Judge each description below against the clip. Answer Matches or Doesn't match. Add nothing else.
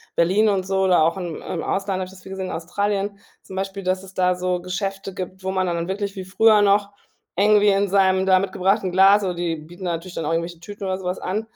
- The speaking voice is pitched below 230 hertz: Matches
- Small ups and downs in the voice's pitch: Matches